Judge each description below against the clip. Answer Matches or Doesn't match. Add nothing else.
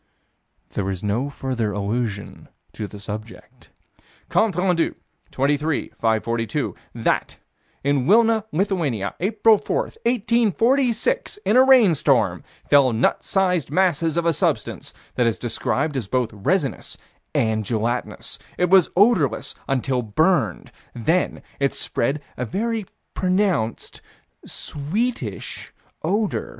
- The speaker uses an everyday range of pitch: Doesn't match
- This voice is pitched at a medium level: Matches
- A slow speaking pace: Matches